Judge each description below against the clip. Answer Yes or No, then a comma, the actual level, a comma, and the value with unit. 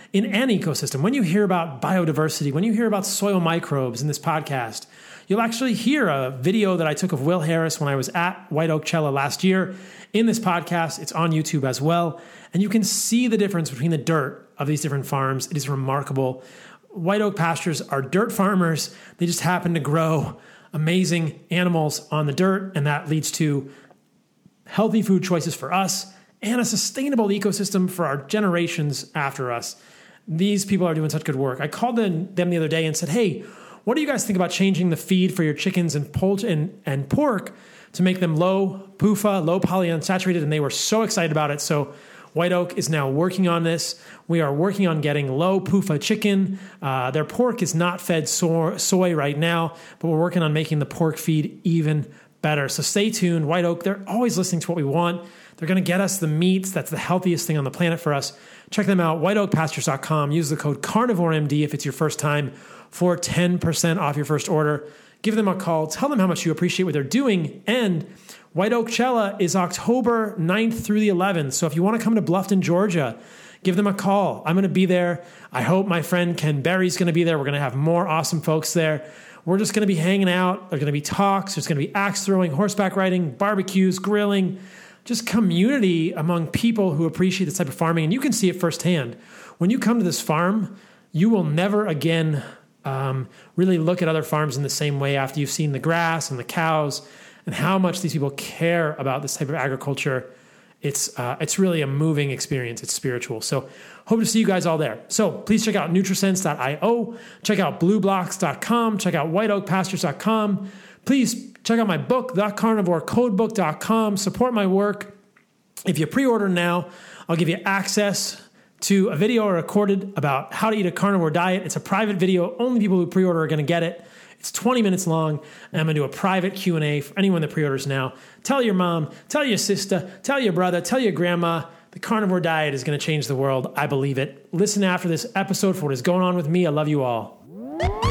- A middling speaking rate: No, fast, 210 wpm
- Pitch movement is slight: No, average, 4.1 semitones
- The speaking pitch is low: No, medium, 175 Hz